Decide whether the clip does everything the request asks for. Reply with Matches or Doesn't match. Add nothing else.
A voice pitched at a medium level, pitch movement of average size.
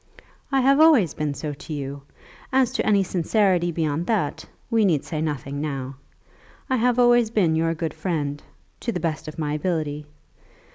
Doesn't match